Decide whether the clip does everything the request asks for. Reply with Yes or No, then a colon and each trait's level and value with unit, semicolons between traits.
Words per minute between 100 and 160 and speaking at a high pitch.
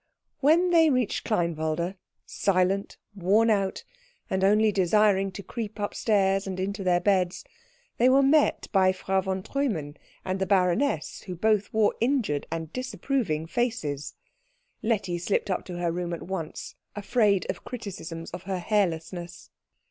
Yes: average, 140 wpm; high, 195 Hz